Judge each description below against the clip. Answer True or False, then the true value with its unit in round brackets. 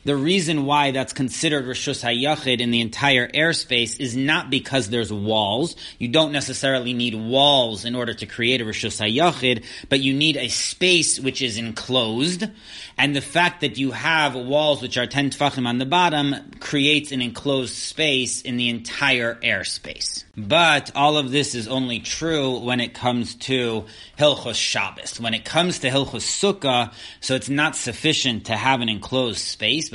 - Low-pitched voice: True (130 Hz)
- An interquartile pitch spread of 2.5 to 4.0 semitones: True (3.4 semitones)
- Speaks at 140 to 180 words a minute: True (170 wpm)